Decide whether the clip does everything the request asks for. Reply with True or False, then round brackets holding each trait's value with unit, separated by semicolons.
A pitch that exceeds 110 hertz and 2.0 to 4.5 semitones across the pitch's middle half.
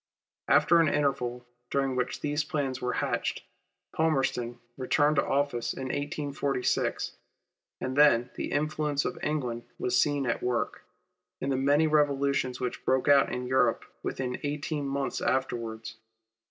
True (135 Hz; 2.7 semitones)